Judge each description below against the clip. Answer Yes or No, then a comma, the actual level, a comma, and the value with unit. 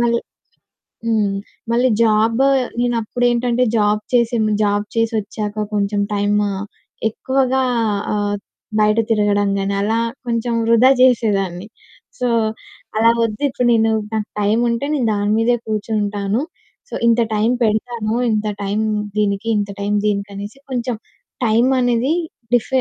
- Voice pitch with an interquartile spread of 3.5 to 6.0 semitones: No, narrow, 2.4 semitones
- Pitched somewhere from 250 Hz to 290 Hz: No, high, 220 Hz